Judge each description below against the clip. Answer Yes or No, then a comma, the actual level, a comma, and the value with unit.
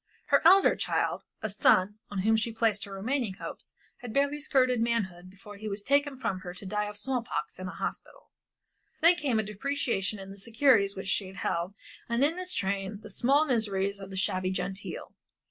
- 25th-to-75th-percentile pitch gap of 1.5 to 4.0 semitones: No, average, 4.6 semitones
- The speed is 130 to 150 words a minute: No, average, 195 wpm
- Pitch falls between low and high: No, high, 210 Hz